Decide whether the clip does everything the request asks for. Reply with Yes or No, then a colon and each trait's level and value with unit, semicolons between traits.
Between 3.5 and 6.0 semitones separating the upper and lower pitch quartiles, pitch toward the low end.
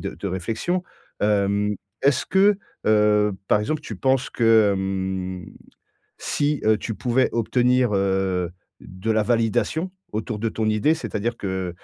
Yes: average, 4.1 semitones; low, 110 Hz